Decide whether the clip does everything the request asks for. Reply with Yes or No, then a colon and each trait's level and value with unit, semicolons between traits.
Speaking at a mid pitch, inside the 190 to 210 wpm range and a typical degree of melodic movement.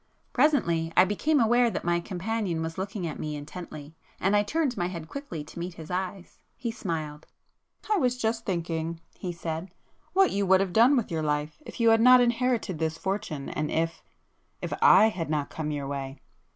No: medium, 180 Hz; average, 195 wpm; wide, 6.0 semitones